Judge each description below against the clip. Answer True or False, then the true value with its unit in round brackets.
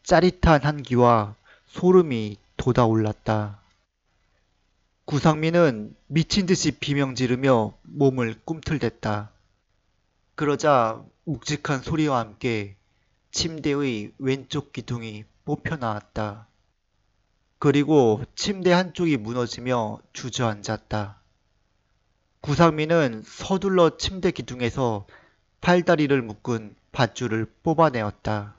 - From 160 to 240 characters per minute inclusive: True (210 characters per minute)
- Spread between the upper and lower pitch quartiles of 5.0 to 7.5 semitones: True (6.0 semitones)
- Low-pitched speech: True (120 Hz)